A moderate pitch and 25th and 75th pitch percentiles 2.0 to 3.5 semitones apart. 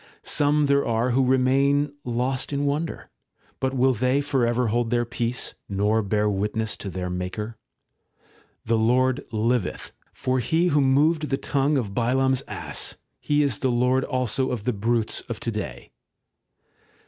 No: low, 125 Hz; average, 3.2 semitones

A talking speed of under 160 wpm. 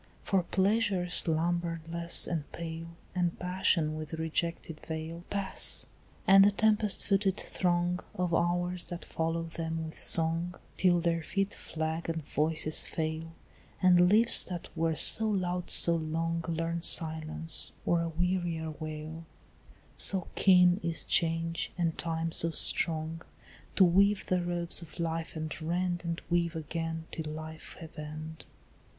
Yes: average, 140 wpm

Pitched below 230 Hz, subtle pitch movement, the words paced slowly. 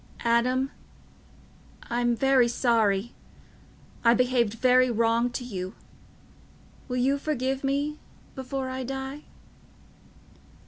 No: very high, 250 Hz; narrow, 2.3 semitones; slow, 95 wpm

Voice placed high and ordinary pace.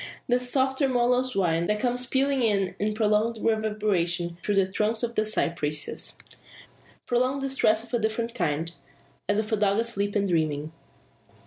Yes: high, 215 Hz; average, 150 wpm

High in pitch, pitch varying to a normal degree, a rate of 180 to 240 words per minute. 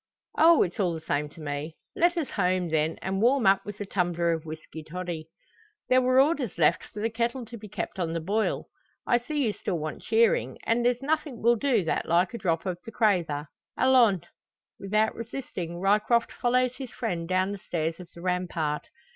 No: high, 195 Hz; wide, 5.9 semitones; average, 200 wpm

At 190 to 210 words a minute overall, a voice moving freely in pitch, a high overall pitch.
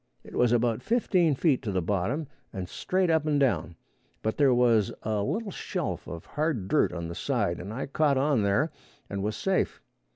No: average, 195 wpm; wide, 7.3 semitones; low, 120 Hz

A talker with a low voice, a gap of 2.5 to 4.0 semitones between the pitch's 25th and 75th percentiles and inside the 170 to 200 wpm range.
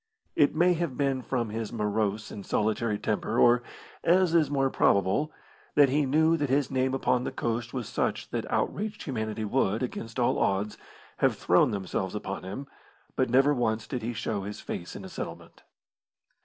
No: low, 120 Hz; average, 4.7 semitones; average, 180 wpm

